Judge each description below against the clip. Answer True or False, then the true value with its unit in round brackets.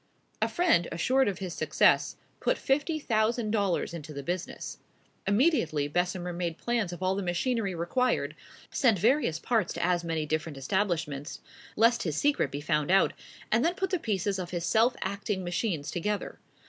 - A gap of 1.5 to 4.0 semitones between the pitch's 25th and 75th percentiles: False (5.4 semitones)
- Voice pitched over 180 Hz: True (190 Hz)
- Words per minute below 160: False (170 wpm)